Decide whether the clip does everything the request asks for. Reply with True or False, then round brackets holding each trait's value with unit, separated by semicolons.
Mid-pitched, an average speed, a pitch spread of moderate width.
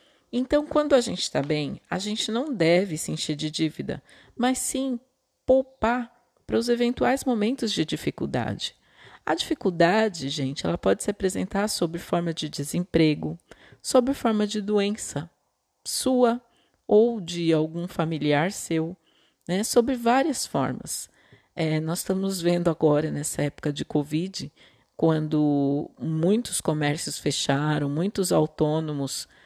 False (175 Hz; 130 wpm; 7.4 semitones)